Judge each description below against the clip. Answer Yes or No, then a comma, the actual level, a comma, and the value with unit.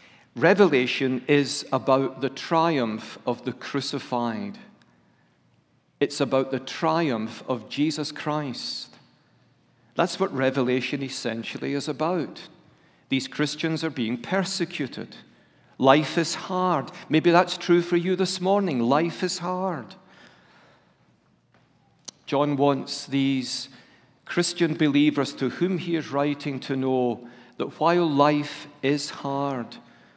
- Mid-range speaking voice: Yes, medium, 145 Hz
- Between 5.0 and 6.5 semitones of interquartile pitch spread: No, average, 3.9 semitones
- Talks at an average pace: No, slow, 110 wpm